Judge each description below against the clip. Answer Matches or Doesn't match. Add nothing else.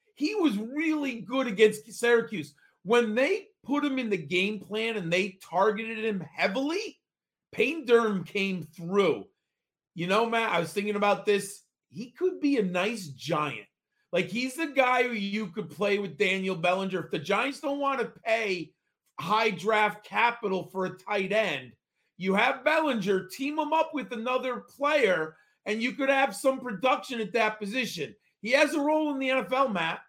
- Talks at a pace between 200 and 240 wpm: Doesn't match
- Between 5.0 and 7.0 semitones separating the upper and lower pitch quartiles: Matches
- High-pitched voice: Matches